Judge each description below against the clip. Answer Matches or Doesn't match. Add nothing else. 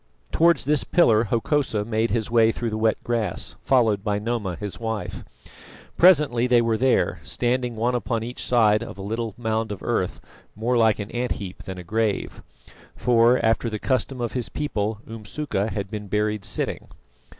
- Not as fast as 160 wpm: Doesn't match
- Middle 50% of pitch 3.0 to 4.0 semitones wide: Doesn't match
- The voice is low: Matches